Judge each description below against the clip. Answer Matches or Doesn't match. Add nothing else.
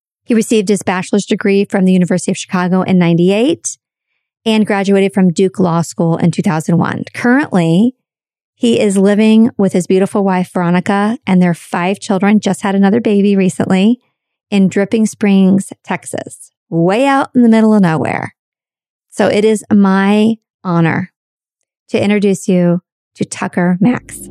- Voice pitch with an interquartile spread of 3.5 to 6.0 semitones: Doesn't match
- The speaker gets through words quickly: Doesn't match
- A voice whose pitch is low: Doesn't match